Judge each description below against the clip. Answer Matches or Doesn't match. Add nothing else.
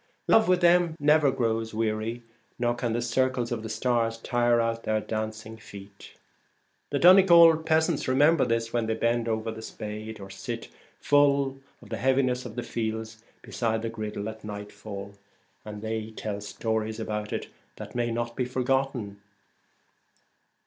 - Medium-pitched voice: Doesn't match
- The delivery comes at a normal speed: Matches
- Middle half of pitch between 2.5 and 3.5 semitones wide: Matches